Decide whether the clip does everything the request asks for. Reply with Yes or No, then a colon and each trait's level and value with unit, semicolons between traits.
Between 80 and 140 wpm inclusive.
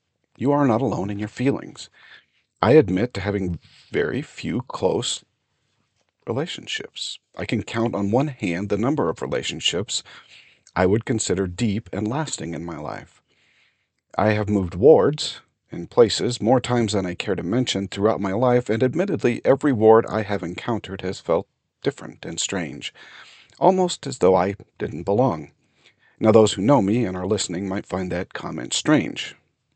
No: average, 165 wpm